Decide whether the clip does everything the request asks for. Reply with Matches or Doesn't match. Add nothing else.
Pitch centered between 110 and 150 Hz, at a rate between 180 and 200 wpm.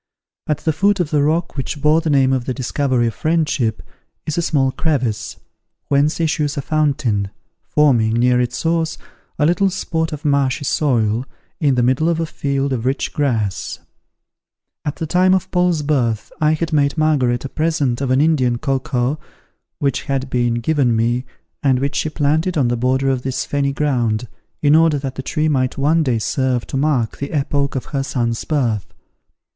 Matches